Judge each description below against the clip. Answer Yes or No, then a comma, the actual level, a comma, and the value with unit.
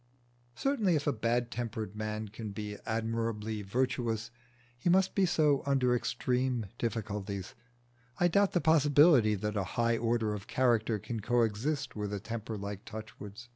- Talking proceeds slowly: No, average, 150 wpm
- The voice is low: Yes, low, 115 Hz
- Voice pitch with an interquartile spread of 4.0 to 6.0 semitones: No, average, 3.6 semitones